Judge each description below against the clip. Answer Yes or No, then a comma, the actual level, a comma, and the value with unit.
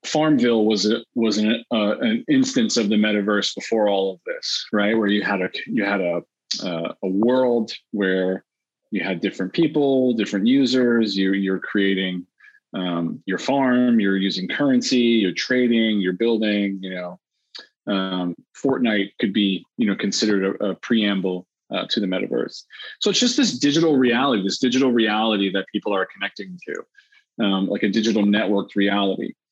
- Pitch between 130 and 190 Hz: No, low, 105 Hz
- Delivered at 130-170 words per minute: Yes, average, 165 wpm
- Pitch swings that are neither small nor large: Yes, average, 4.2 semitones